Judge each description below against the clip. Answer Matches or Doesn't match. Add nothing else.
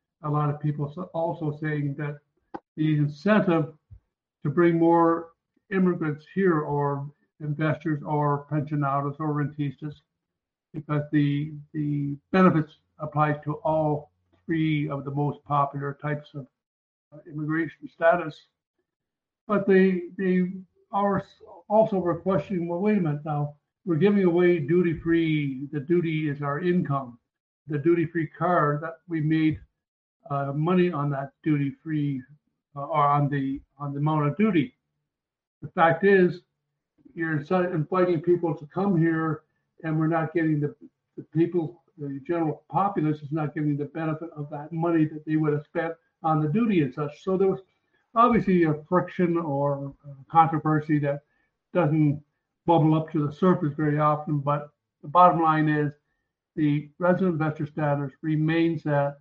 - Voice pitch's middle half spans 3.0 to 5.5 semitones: Doesn't match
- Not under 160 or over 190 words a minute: Doesn't match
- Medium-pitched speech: Matches